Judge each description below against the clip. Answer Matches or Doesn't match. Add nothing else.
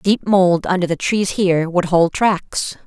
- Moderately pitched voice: Matches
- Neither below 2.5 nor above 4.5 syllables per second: Matches